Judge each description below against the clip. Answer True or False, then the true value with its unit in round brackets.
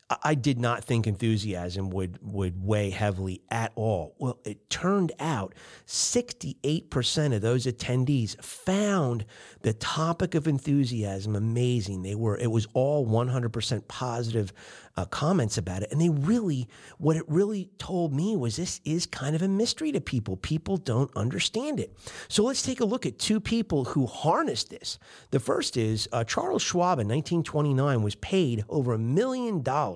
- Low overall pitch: True (130 Hz)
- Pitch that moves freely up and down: True (6.7 semitones)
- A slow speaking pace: False (170 wpm)